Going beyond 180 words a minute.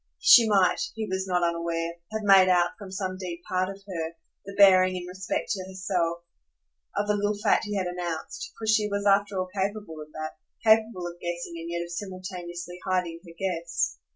Yes: average, 195 wpm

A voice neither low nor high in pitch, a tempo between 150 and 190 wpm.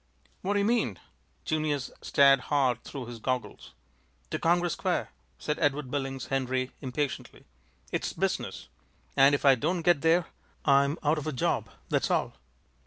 Yes: medium, 145 Hz; average, 155 wpm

